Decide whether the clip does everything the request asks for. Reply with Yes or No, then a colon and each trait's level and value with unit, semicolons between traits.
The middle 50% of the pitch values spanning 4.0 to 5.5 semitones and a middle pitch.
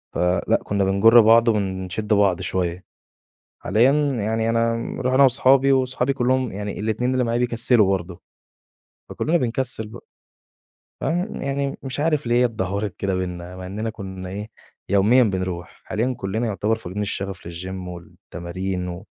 No: average, 4.5 semitones; low, 105 Hz